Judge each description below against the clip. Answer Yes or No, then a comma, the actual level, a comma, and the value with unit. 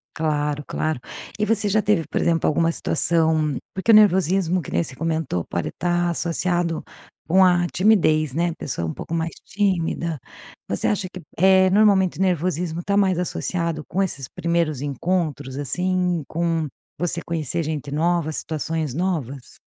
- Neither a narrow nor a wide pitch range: Yes, average, 3.0 semitones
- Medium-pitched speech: Yes, medium, 170 Hz